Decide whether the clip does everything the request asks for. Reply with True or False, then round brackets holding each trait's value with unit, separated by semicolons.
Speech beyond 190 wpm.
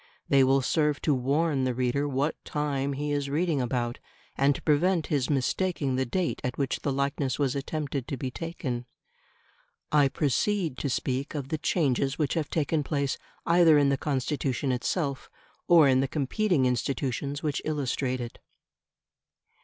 False (160 wpm)